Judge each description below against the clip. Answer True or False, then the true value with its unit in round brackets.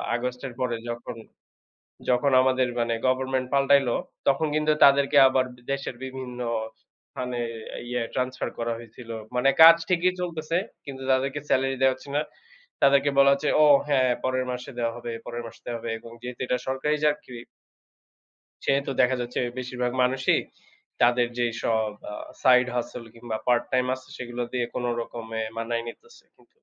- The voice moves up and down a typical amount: False (2.2 semitones)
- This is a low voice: True (125 Hz)